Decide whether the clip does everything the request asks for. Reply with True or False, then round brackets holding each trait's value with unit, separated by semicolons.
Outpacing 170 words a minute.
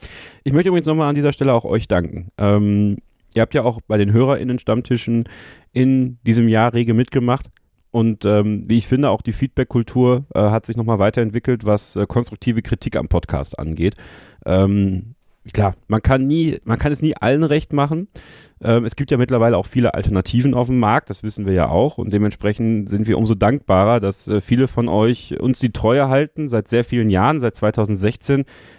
True (190 wpm)